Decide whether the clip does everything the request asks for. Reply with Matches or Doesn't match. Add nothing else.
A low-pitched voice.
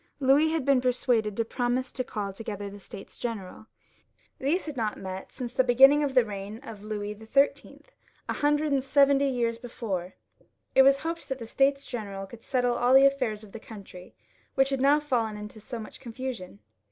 Doesn't match